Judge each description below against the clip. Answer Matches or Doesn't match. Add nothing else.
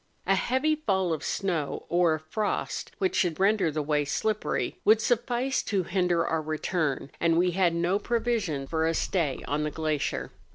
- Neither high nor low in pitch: Matches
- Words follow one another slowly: Doesn't match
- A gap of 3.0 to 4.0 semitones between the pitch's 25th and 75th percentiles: Doesn't match